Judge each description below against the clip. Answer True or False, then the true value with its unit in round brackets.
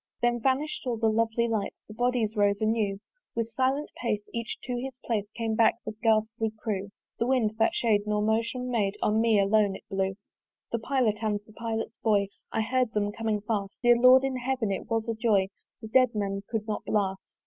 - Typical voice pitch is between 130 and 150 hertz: False (225 Hz)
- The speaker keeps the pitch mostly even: True (2.3 semitones)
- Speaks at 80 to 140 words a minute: False (205 wpm)